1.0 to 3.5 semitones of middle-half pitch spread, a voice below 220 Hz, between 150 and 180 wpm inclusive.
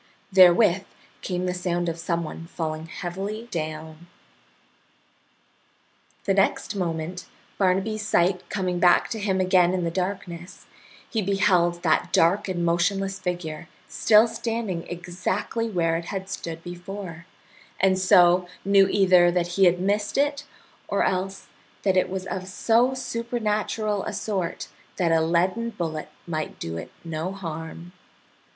No: average, 2.7 semitones; medium, 185 Hz; average, 140 wpm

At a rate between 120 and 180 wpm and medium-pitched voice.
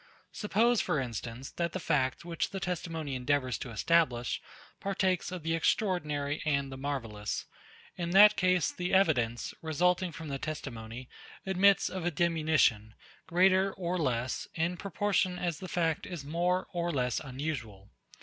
Yes: average, 150 wpm; medium, 165 Hz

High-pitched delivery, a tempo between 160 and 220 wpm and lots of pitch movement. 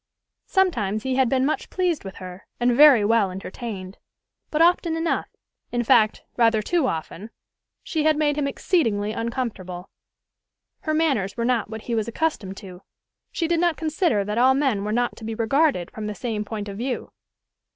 Yes: high, 235 Hz; average, 180 wpm; wide, 6.4 semitones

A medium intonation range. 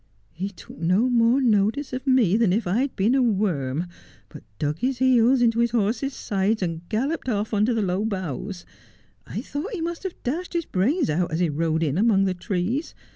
No: wide, 5.9 semitones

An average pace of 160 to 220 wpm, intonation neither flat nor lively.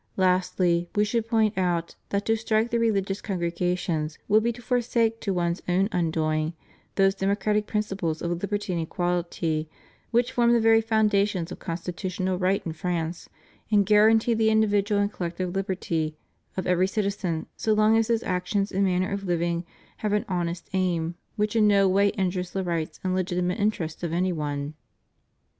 Yes: average, 170 wpm; average, 3.4 semitones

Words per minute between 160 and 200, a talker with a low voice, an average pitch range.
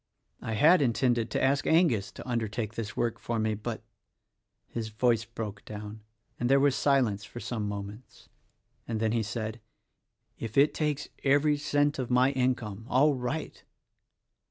Yes: average, 170 wpm; low, 120 Hz; average, 4.0 semitones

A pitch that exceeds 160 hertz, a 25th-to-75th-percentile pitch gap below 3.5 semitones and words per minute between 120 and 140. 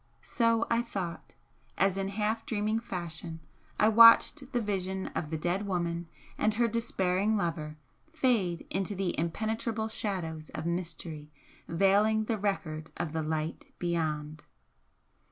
No: high, 190 Hz; average, 4.7 semitones; slow, 135 wpm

